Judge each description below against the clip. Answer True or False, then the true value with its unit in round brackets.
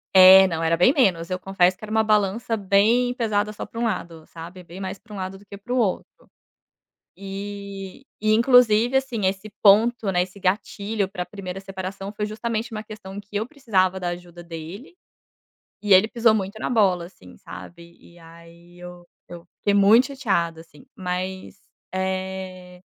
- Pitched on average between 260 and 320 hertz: False (195 Hz)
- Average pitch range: True (3.1 semitones)